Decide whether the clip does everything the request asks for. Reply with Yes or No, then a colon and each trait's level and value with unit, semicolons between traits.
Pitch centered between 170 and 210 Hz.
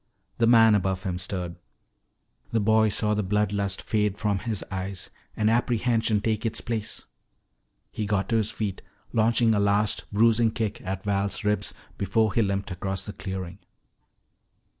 No: low, 105 Hz